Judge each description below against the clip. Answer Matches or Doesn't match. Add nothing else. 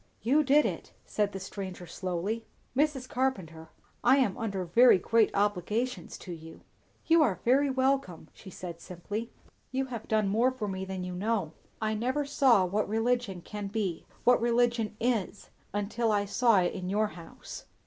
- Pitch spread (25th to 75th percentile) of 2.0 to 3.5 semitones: Doesn't match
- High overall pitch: Matches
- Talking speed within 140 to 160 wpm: Doesn't match